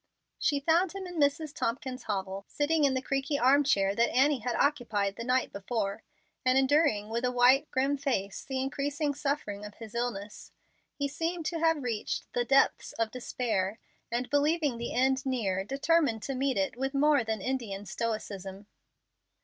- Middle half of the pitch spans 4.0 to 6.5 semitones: Yes, average, 4.6 semitones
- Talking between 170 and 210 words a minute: Yes, average, 175 wpm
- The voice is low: No, very high, 255 Hz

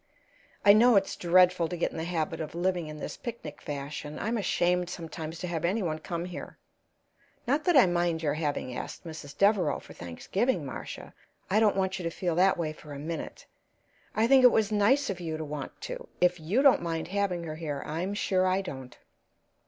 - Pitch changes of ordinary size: Yes, average, 4.1 semitones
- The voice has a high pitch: No, medium, 175 Hz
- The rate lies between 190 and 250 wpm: Yes, fast, 205 wpm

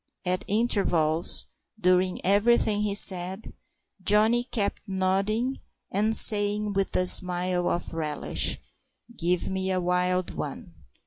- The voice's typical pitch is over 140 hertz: Yes, high, 190 Hz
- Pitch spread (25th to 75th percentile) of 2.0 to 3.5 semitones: Yes, narrow, 2.6 semitones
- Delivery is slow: Yes, slow, 115 wpm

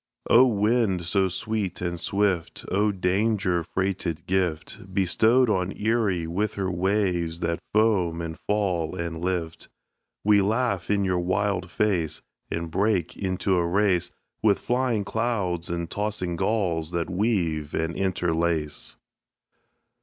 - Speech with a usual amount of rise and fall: Yes, average, 3.4 semitones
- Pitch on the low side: Yes, very low, 95 Hz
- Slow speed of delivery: Yes, slow, 130 wpm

